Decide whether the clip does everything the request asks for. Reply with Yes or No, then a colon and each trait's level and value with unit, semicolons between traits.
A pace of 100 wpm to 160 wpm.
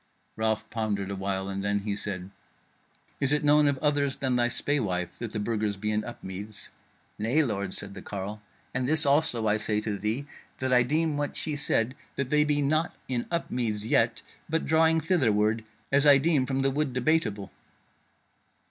No: average, 185 wpm